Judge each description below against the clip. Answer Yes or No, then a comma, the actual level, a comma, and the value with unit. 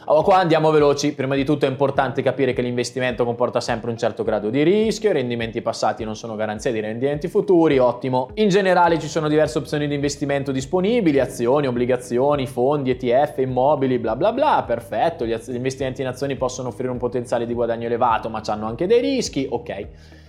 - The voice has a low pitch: Yes, low, 130 Hz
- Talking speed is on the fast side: Yes, fast, 190 wpm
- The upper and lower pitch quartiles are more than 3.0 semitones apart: Yes, average, 3.5 semitones